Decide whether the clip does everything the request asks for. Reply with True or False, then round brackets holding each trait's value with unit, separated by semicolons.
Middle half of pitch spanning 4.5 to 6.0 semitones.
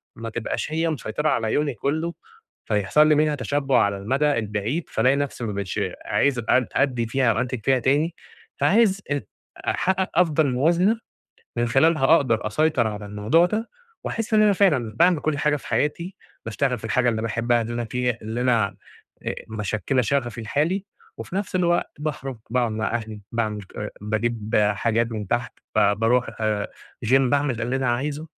True (5.3 semitones)